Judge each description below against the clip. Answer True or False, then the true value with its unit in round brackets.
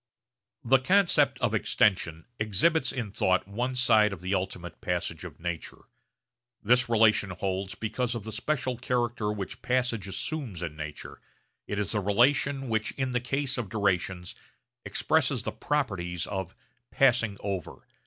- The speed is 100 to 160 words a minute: True (145 wpm)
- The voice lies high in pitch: False (105 Hz)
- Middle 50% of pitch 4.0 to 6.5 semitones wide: True (5.0 semitones)